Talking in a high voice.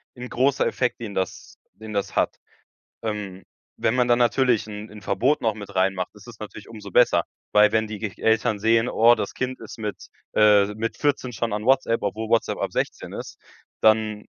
No: low, 110 Hz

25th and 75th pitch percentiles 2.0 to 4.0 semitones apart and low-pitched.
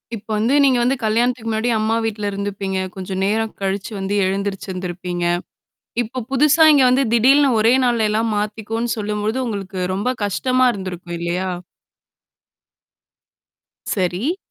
No: average, 3.7 semitones; high, 215 Hz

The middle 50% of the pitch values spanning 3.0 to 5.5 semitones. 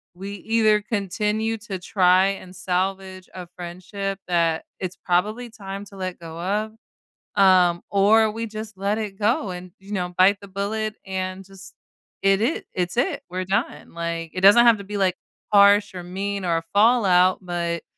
No: narrow, 2.5 semitones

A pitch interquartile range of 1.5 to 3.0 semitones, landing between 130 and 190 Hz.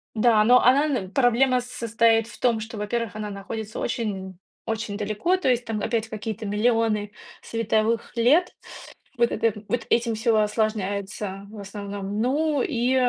No: narrow, 2.4 semitones; high, 225 Hz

